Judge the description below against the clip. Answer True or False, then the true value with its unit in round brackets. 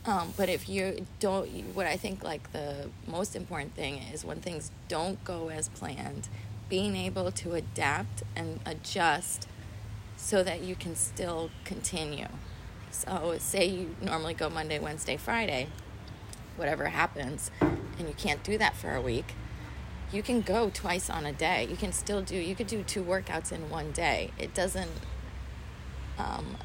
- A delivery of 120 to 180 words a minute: True (160 wpm)